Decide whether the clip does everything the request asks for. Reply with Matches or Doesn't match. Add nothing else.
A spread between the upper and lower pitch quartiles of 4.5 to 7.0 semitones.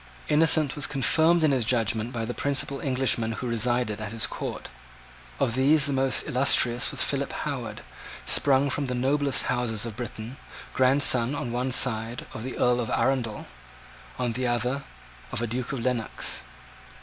Doesn't match